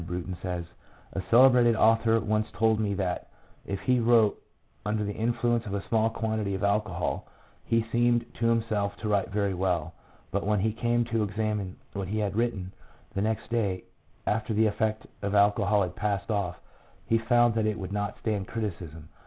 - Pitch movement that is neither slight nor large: No, narrow, 2.3 semitones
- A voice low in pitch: Yes, low, 105 Hz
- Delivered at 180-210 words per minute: Yes, average, 185 wpm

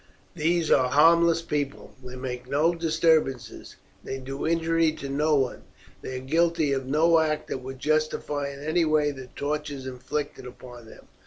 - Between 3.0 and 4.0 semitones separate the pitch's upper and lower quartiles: Yes, average, 3.3 semitones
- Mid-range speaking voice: Yes, medium, 150 Hz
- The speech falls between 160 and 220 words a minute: Yes, average, 165 wpm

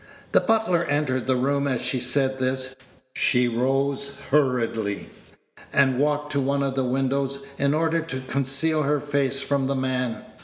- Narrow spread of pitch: Yes, narrow, 1.6 semitones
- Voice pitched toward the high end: No, low, 135 Hz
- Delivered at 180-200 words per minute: No, average, 160 wpm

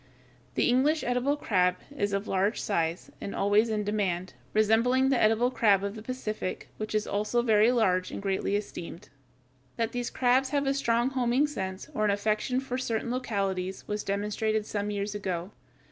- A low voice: No, high, 215 Hz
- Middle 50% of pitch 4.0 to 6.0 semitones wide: No, average, 3.6 semitones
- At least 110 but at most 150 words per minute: No, average, 175 wpm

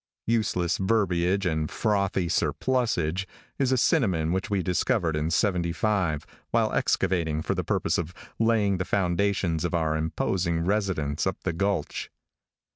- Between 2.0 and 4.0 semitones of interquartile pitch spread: Yes, average, 3.5 semitones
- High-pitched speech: No, very low, 90 Hz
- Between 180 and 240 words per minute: No, slow, 135 wpm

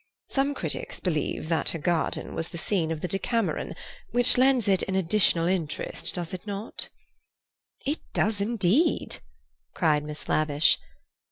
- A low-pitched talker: No, medium, 185 Hz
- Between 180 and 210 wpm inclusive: No, average, 145 wpm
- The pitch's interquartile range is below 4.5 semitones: No, wide, 5.4 semitones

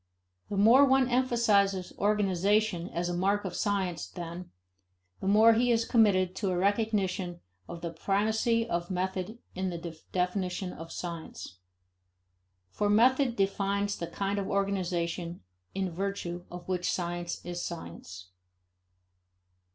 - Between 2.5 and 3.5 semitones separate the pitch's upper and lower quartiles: Yes, average, 2.9 semitones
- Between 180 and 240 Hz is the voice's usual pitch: Yes, high, 190 Hz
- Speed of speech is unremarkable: No, slow, 130 wpm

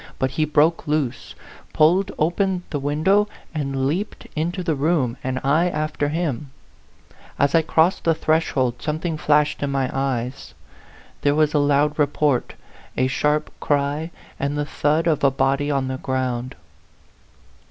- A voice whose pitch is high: No, medium, 150 Hz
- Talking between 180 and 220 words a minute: No, average, 150 wpm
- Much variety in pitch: No, narrow, 2.6 semitones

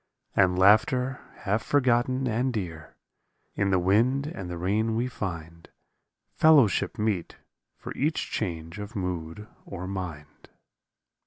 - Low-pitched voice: Yes, low, 100 Hz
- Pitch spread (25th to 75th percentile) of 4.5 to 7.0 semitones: Yes, average, 5.3 semitones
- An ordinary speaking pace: No, slow, 125 wpm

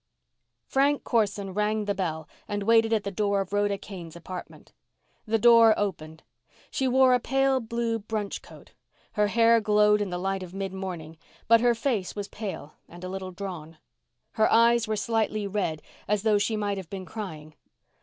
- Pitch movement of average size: Yes, average, 3.1 semitones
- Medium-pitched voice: No, high, 205 Hz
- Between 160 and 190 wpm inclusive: Yes, average, 175 wpm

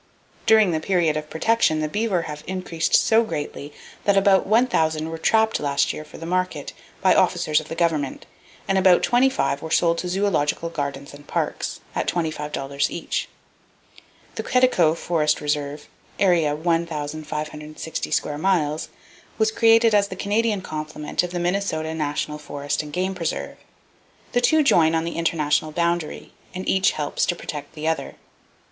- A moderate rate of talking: Yes, average, 155 wpm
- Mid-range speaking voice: Yes, medium, 165 Hz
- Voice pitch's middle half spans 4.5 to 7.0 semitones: No, average, 3.9 semitones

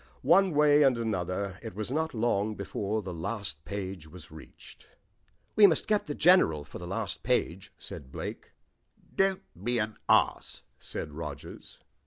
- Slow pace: No, average, 155 wpm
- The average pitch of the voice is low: Yes, low, 105 Hz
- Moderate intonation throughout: No, wide, 8.7 semitones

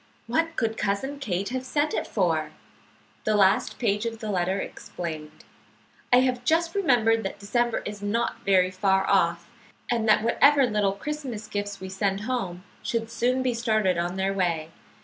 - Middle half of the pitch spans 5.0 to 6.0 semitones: No, average, 4.2 semitones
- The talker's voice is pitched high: Yes, high, 210 Hz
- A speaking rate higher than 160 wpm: Yes, average, 170 wpm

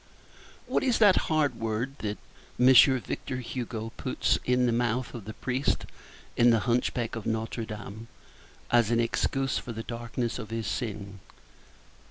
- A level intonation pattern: Yes, narrow, 2.2 semitones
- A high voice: No, low, 120 Hz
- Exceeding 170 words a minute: No, average, 155 wpm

